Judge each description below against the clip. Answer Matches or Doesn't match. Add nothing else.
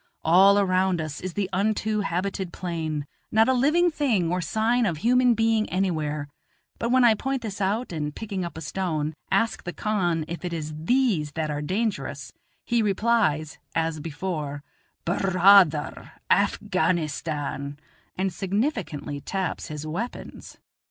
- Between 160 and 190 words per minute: Doesn't match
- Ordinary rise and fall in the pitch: Doesn't match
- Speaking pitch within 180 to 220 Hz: Matches